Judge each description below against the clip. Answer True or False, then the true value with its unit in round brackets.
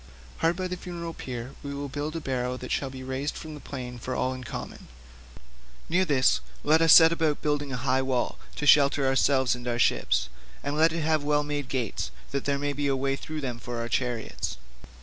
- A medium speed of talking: False (220 wpm)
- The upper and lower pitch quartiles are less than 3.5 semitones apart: True (2.9 semitones)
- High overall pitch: False (140 Hz)